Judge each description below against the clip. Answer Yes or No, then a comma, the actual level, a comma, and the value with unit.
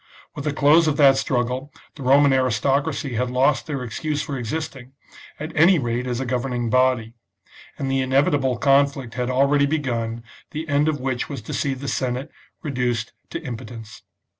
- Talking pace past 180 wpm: No, average, 170 wpm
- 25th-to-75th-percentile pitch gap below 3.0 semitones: Yes, narrow, 2.5 semitones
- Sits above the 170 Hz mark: No, low, 135 Hz